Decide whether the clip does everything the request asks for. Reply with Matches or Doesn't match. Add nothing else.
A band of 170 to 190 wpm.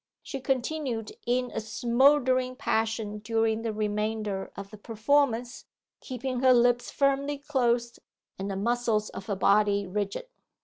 Doesn't match